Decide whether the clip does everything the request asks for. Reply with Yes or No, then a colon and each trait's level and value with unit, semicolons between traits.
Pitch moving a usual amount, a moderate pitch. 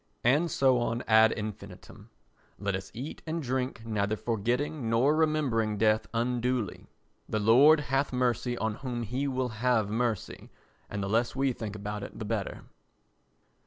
No: average, 3.2 semitones; low, 120 Hz